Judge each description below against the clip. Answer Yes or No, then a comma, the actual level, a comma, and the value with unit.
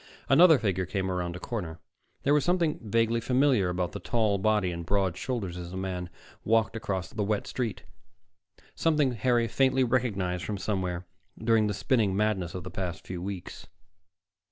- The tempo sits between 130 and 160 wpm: No, average, 170 wpm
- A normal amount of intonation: Yes, average, 4.7 semitones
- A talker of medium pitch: No, low, 105 Hz